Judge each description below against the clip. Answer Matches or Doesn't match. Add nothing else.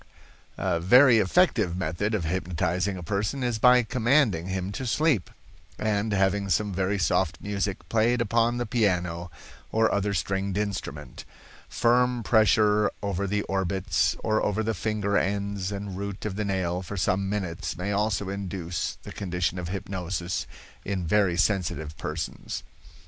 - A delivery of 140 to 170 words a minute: Matches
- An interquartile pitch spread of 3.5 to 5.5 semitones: Doesn't match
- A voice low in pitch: Matches